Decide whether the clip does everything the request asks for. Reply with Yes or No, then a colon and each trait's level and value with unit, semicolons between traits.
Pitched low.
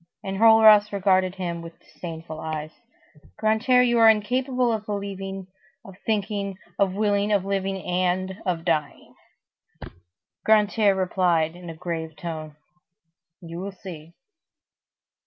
No: high, 190 Hz